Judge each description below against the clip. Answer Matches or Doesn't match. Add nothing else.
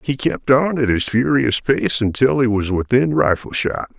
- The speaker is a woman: Doesn't match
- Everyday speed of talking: Matches